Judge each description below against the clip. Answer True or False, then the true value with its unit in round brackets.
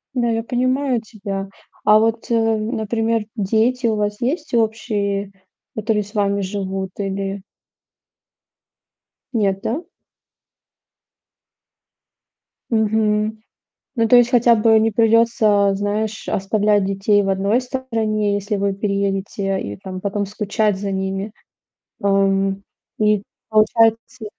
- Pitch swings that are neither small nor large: False (2.3 semitones)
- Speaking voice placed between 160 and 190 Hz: False (210 Hz)